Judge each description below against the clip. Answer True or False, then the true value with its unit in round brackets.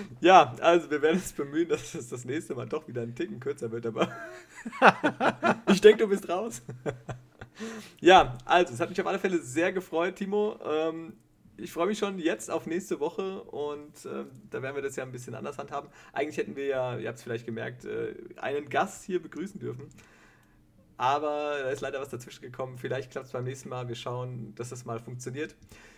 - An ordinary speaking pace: False (200 wpm)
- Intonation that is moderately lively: False (6.8 semitones)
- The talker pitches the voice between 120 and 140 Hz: False (150 Hz)